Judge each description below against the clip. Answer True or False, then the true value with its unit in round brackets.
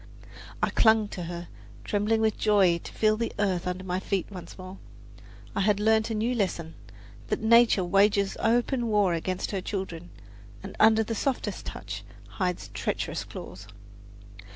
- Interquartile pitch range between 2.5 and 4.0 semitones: True (3.2 semitones)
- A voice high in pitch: True (200 Hz)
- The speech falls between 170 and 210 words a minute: False (155 wpm)